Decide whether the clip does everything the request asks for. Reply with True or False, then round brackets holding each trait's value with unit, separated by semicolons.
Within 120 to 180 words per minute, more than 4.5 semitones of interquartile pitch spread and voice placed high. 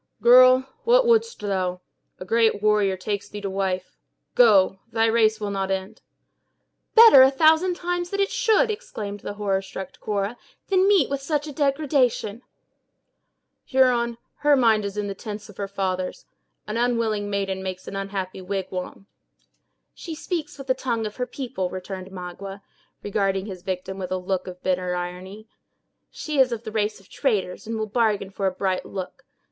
True (170 wpm; 5.1 semitones; 210 Hz)